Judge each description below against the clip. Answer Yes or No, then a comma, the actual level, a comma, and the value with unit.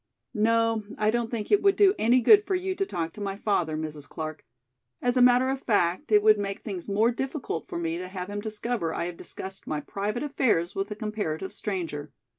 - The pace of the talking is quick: Yes, fast, 220 wpm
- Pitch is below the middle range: No, high, 210 Hz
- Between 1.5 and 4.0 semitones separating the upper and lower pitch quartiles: No, wide, 5.4 semitones